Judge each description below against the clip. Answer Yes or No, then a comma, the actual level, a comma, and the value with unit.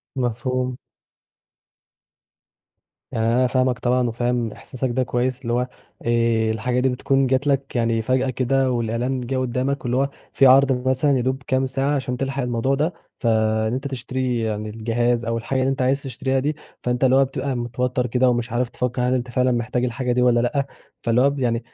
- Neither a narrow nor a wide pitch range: No, narrow, 1.7 semitones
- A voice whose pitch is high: No, low, 125 Hz